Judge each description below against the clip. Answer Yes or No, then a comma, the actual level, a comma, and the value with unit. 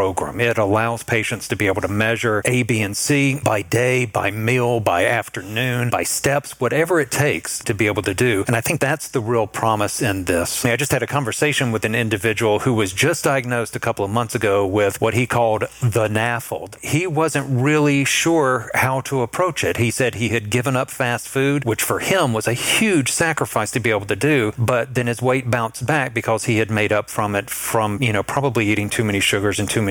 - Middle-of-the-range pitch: No, low, 120 Hz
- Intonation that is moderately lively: Yes, average, 3.0 semitones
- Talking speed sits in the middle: No, fast, 230 wpm